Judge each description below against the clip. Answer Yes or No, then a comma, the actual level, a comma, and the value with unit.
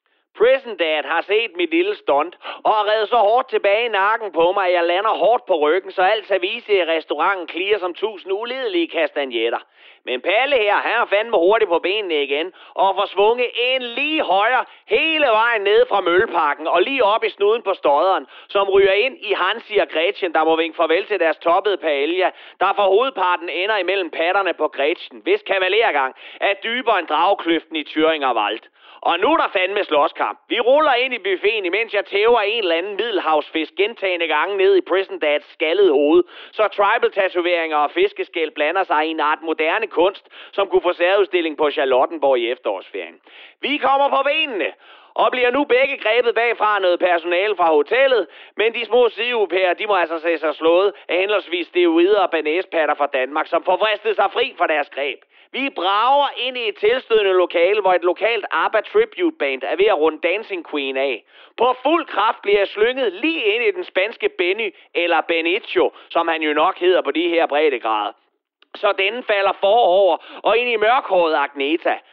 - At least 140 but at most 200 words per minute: Yes, average, 190 wpm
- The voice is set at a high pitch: Yes, high, 215 Hz